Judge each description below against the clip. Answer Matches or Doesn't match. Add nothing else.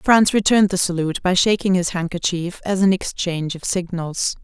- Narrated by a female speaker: Matches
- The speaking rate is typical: Matches